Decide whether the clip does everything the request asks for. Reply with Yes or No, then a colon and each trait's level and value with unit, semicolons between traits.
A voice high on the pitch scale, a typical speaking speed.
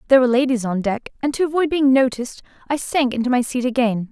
No: very high, 255 Hz; fast, 235 wpm